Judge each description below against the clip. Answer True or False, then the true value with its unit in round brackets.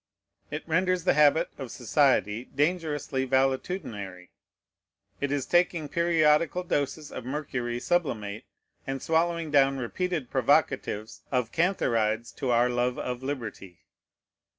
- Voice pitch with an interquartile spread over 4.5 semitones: True (5.0 semitones)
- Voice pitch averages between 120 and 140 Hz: True (135 Hz)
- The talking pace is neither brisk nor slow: False (115 wpm)